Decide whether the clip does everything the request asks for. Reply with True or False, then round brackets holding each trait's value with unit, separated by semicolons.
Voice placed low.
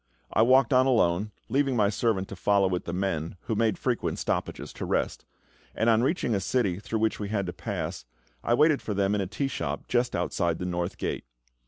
True (105 Hz)